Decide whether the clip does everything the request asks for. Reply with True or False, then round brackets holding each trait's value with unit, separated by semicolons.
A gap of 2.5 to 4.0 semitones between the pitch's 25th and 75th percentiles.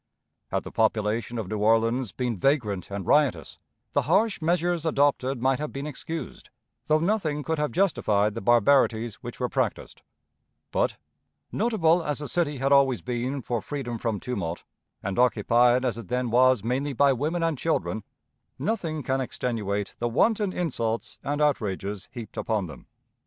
False (5.0 semitones)